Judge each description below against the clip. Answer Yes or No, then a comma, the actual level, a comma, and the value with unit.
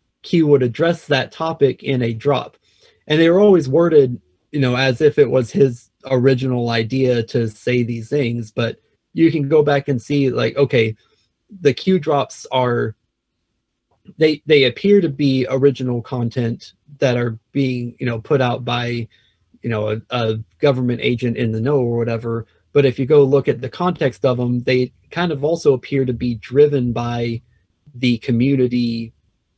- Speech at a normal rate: Yes, average, 175 wpm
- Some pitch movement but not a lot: Yes, average, 3.5 semitones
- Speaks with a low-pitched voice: Yes, low, 125 Hz